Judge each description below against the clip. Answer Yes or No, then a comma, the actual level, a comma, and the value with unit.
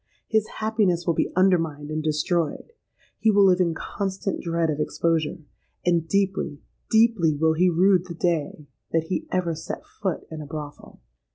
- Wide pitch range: No, average, 3.2 semitones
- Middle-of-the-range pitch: Yes, medium, 170 Hz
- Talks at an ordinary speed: Yes, average, 160 wpm